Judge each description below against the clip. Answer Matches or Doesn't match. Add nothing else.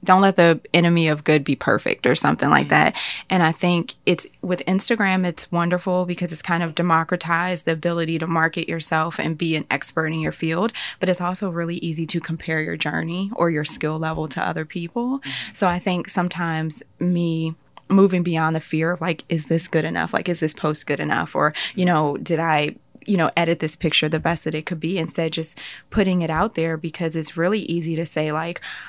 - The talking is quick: Matches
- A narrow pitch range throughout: Matches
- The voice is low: Doesn't match